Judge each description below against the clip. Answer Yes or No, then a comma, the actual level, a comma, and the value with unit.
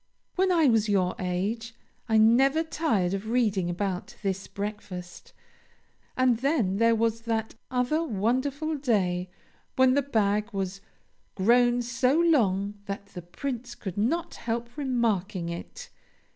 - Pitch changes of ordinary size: Yes, average, 4.5 semitones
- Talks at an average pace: No, slow, 130 wpm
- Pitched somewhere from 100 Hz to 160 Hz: No, high, 225 Hz